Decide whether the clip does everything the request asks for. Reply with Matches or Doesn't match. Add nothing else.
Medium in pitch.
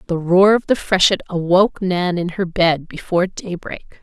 Matches